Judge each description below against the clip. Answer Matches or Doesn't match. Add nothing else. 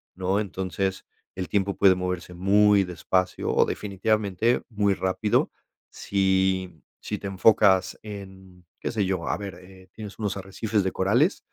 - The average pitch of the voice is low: Matches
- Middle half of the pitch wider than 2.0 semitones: Doesn't match